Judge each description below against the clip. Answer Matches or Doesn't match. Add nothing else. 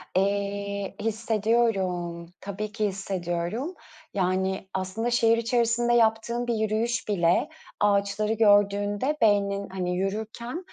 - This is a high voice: Matches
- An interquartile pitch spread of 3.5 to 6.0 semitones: Doesn't match